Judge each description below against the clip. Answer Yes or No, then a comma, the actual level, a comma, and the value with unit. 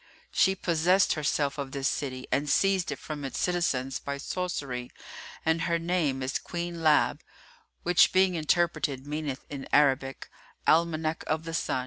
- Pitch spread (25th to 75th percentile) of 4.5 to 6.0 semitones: No, average, 3.6 semitones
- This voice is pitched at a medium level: Yes, medium, 155 Hz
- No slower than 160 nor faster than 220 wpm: No, average, 150 wpm